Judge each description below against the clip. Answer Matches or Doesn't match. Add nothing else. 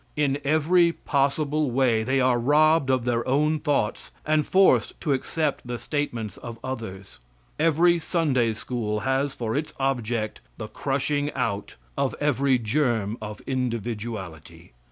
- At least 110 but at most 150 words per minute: Matches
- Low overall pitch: Matches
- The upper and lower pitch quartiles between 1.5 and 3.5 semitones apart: Doesn't match